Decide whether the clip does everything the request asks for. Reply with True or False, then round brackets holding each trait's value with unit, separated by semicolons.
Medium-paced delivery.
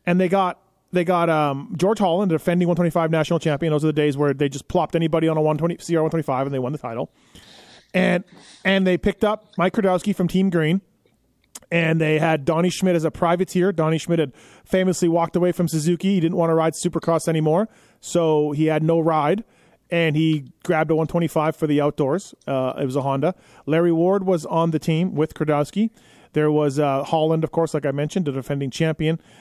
False (210 wpm)